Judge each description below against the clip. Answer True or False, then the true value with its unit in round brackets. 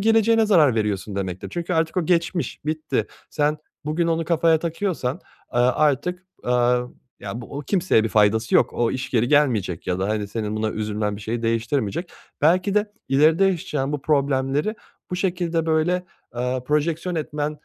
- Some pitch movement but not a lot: False (6.7 semitones)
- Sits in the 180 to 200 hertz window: False (150 Hz)